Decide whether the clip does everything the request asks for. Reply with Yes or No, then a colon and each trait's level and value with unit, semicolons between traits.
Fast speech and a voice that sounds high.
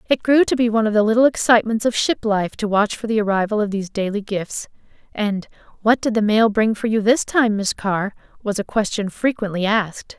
Yes: fast, 225 wpm; high, 215 Hz